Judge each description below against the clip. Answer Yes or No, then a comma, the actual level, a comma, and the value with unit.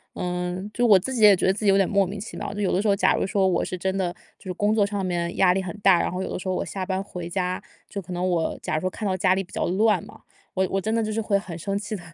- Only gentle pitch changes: Yes, narrow, 2.0 semitones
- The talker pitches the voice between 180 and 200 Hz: Yes, high, 190 Hz